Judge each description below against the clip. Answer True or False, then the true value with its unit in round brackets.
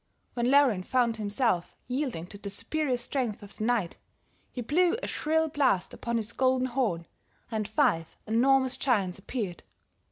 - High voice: True (240 Hz)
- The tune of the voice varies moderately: True (4.5 semitones)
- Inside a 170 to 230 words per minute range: False (155 wpm)